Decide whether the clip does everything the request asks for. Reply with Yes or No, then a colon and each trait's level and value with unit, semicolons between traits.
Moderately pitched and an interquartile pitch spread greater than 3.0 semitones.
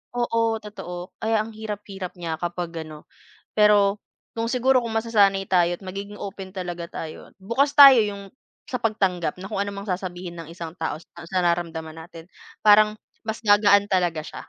No: high, 195 Hz; average, 3.5 semitones